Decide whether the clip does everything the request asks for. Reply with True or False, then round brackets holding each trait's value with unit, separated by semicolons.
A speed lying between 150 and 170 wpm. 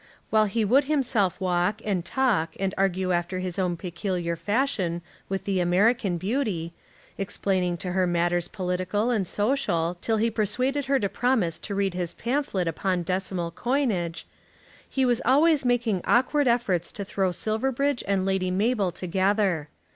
True (155 wpm)